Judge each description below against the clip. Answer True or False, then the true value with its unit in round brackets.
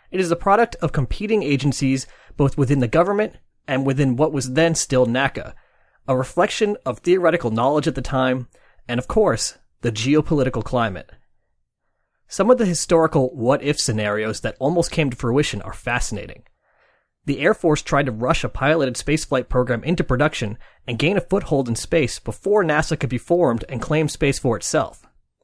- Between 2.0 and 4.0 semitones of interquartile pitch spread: False (4.7 semitones)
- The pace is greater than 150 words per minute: True (170 wpm)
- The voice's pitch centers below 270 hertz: True (140 Hz)